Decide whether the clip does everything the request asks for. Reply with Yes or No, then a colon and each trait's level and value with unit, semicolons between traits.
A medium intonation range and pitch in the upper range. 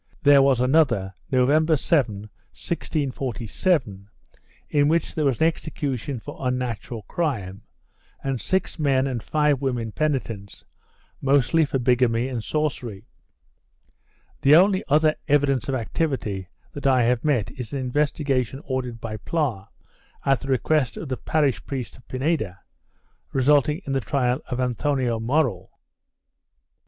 No: average, 3.8 semitones; low, 130 Hz